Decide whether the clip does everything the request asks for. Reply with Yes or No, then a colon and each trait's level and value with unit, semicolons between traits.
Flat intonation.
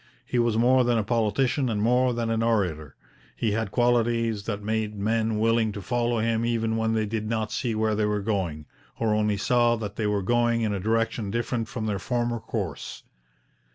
Yes: narrow, 1.9 semitones